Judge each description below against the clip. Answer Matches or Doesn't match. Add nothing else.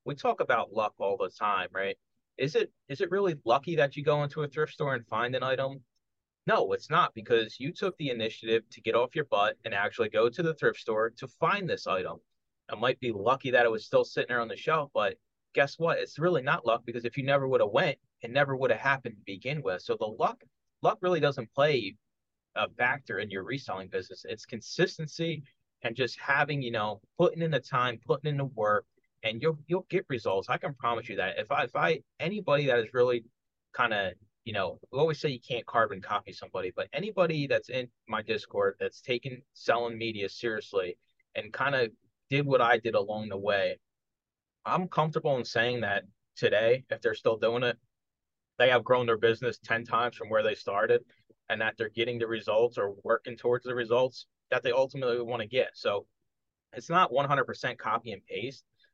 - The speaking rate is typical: Doesn't match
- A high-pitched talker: Doesn't match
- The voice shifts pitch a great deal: Matches